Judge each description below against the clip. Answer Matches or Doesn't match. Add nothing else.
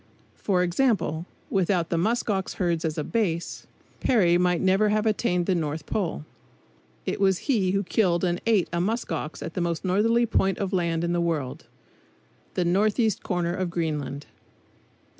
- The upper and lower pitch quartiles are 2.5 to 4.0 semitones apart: Matches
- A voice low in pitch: Doesn't match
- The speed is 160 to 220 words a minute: Matches